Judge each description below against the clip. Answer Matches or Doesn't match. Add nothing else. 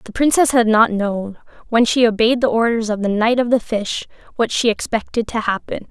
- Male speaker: Doesn't match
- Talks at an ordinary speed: Doesn't match